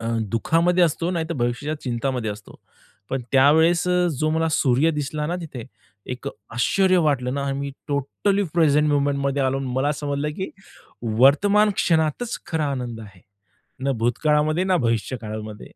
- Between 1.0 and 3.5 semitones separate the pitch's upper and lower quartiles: No, average, 4.4 semitones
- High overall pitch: No, medium, 145 Hz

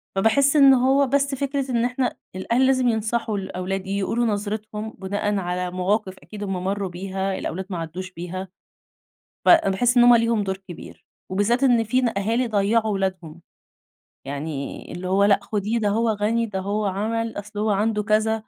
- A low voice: No, high, 210 Hz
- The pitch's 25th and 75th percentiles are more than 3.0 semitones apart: Yes, average, 3.4 semitones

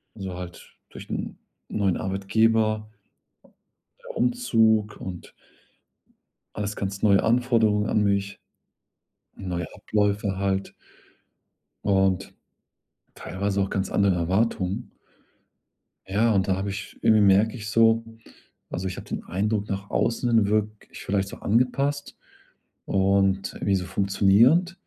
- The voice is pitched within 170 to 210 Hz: No, low, 100 Hz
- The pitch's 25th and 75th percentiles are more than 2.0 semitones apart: Yes, narrow, 2.4 semitones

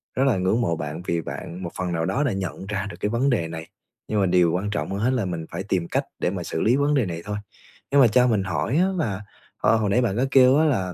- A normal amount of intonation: No, wide, 5.7 semitones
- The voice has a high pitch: No, low, 100 Hz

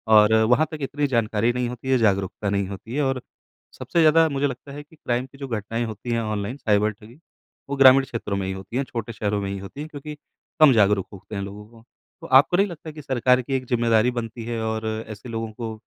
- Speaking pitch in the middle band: No, low, 115 Hz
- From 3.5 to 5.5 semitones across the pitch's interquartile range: Yes, average, 4.2 semitones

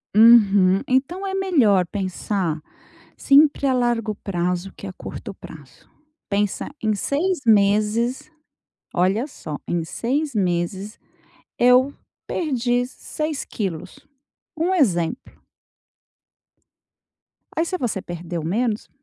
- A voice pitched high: Yes, high, 220 Hz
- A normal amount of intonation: No, wide, 6.4 semitones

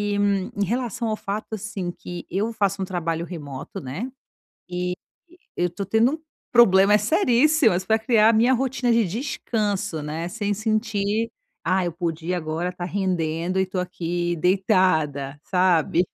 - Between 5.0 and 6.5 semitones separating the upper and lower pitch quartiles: No, average, 3.9 semitones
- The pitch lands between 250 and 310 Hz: No, high, 190 Hz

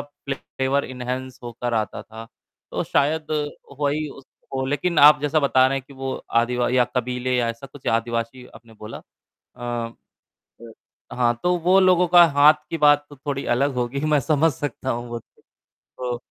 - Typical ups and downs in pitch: Yes, average, 3.3 semitones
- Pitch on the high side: No, low, 130 Hz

